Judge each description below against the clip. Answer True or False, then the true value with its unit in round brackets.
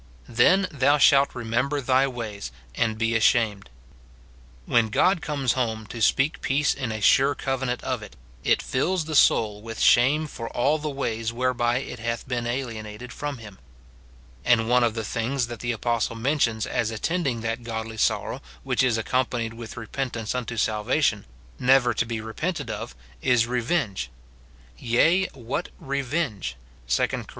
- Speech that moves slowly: False (160 wpm)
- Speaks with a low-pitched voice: True (120 Hz)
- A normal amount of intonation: True (3.2 semitones)